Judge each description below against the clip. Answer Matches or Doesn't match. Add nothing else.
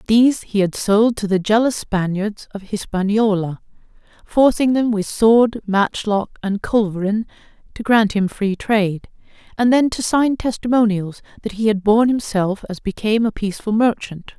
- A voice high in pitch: Matches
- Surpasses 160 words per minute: Doesn't match